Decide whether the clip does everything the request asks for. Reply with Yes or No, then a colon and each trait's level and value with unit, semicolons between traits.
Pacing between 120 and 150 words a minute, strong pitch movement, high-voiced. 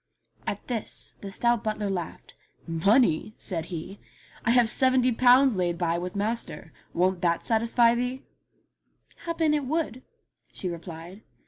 Yes: average, 140 wpm; wide, 5.9 semitones; high, 215 Hz